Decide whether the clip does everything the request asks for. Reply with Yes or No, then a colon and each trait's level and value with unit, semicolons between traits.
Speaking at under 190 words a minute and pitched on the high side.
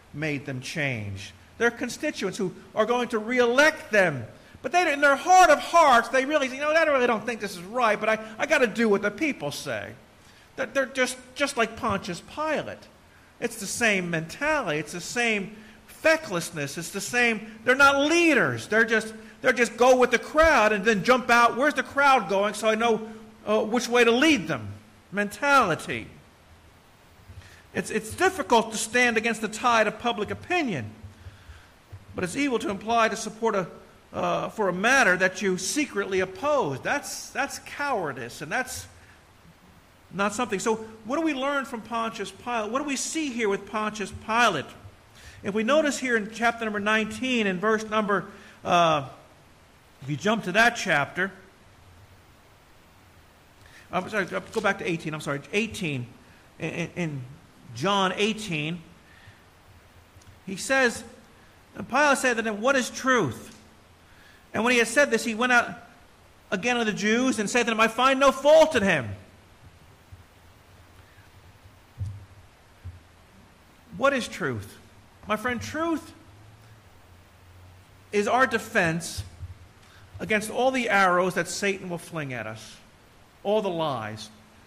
Yes: average, 155 wpm; high, 205 Hz